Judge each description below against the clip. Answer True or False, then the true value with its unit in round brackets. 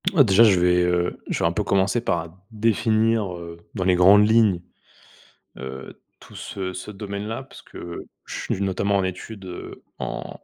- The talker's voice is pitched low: True (95 Hz)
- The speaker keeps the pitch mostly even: False (3.4 semitones)